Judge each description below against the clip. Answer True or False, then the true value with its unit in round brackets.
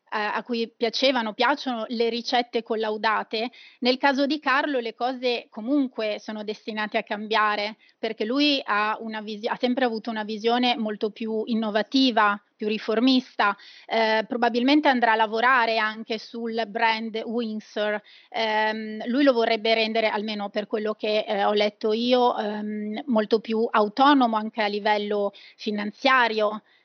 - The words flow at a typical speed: True (140 wpm)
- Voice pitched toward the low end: False (225 Hz)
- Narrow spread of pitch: True (2.1 semitones)